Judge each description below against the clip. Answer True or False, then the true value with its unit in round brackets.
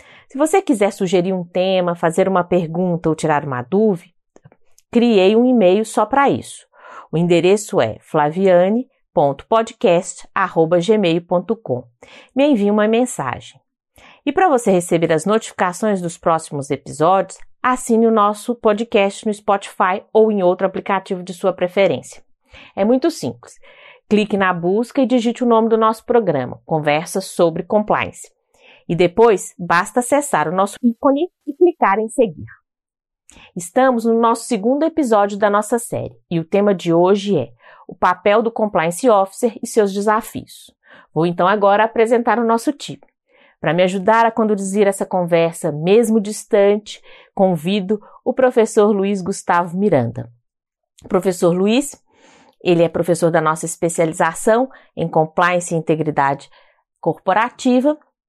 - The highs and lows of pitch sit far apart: False (4.9 semitones)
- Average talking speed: True (135 wpm)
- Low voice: False (200 Hz)